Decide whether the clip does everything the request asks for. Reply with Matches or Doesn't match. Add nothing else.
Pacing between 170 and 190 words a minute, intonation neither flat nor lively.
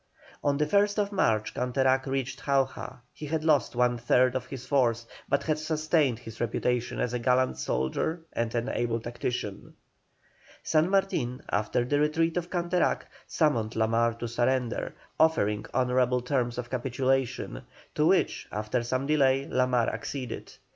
Doesn't match